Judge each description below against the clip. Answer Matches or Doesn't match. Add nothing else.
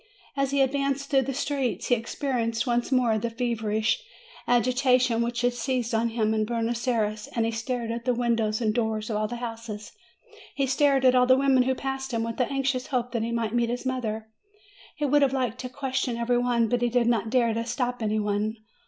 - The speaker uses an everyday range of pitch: Doesn't match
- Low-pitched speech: Doesn't match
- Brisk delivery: Matches